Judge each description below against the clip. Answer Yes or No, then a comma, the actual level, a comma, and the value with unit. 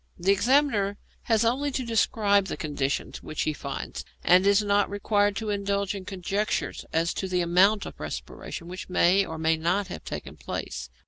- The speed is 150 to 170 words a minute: No, average, 180 wpm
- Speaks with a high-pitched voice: Yes, high, 200 Hz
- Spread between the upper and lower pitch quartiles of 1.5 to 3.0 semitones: Yes, narrow, 2.6 semitones